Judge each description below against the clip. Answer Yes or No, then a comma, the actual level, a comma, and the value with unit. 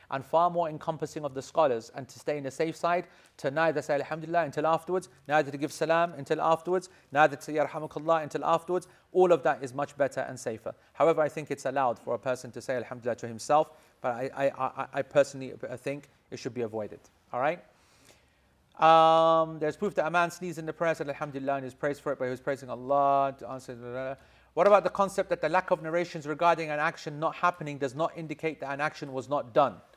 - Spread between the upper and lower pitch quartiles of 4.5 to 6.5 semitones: No, average, 3.1 semitones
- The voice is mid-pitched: Yes, medium, 155 Hz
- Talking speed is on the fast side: Yes, fast, 225 wpm